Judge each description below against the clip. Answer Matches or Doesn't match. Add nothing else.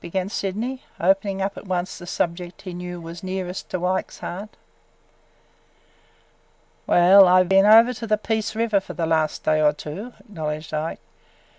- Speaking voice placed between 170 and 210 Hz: Matches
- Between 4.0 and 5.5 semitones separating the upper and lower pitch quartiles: Doesn't match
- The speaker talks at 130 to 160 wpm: Matches